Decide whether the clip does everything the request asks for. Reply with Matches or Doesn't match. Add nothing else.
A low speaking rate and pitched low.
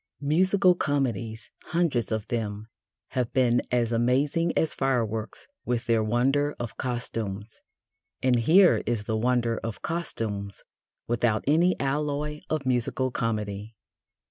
Matches